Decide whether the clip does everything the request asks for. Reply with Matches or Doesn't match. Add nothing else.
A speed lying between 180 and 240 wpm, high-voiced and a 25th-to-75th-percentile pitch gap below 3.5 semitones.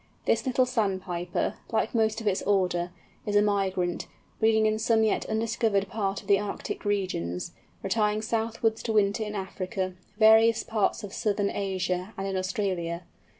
Doesn't match